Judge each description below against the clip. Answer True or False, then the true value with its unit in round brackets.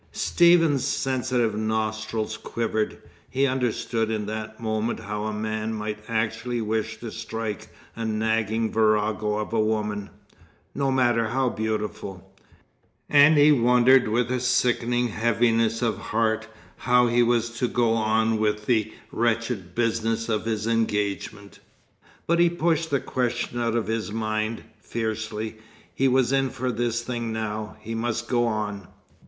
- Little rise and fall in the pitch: True (2.0 semitones)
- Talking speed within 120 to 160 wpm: True (145 wpm)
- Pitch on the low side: True (115 Hz)